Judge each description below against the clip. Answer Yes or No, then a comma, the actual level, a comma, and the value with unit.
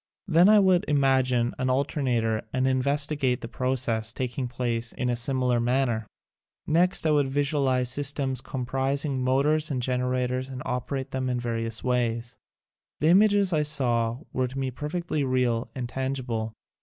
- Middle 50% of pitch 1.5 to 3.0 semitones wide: Yes, narrow, 2.5 semitones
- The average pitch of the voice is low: Yes, low, 130 Hz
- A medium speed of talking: Yes, average, 155 wpm